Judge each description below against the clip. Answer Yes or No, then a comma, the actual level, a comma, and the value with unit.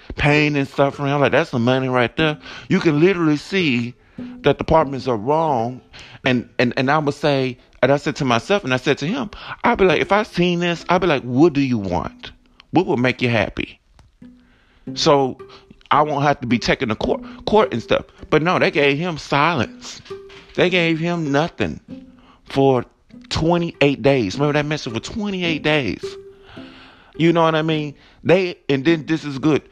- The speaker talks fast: No, average, 195 wpm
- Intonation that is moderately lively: Yes, average, 4.7 semitones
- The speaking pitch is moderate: Yes, medium, 150 Hz